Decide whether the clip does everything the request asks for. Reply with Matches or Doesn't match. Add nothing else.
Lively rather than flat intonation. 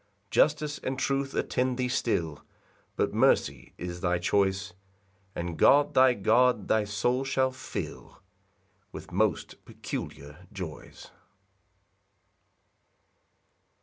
Matches